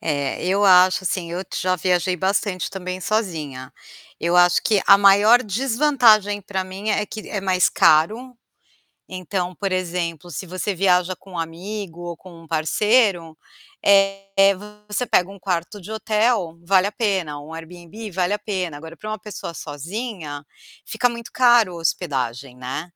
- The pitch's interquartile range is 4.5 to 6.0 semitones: No, average, 3.6 semitones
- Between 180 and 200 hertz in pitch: Yes, medium, 185 Hz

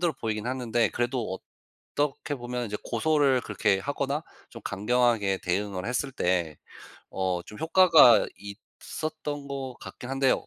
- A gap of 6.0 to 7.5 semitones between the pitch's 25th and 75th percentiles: No, average, 5.3 semitones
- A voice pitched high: No, low, 120 Hz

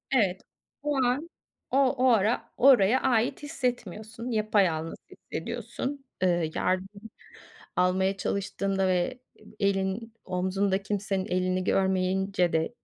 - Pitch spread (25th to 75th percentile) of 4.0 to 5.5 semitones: Yes, average, 4.3 semitones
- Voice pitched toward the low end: No, high, 195 Hz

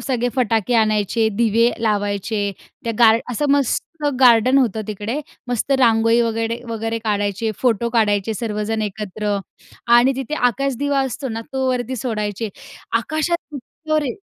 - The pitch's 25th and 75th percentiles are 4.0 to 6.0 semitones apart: No, average, 3.0 semitones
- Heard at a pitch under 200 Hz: No, high, 230 Hz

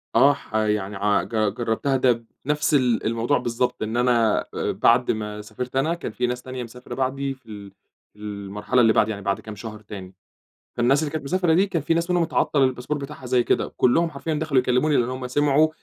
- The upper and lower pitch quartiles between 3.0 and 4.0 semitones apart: No, average, 4.6 semitones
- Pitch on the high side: No, low, 125 Hz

